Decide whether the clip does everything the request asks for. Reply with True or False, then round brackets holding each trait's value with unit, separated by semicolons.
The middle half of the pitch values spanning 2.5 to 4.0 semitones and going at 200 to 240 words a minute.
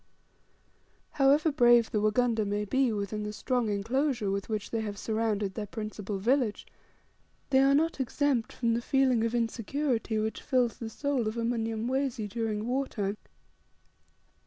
False (3.5 semitones; 155 wpm)